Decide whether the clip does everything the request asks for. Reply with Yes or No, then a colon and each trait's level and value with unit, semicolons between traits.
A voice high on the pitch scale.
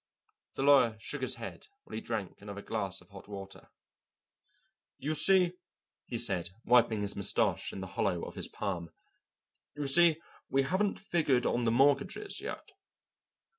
No: low, 115 Hz